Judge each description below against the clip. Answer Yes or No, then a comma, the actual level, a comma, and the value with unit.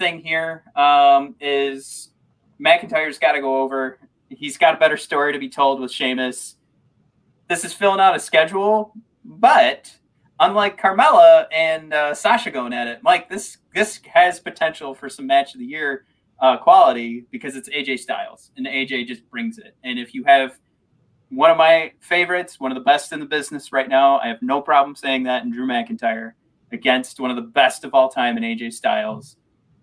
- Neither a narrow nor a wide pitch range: No, wide, 9.0 semitones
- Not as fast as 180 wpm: No, average, 185 wpm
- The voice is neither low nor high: Yes, medium, 160 Hz